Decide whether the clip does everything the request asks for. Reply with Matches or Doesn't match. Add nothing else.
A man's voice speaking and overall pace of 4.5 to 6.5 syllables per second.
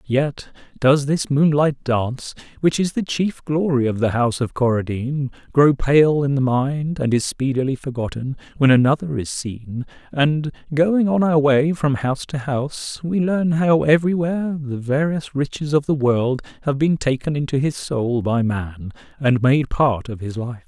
Matches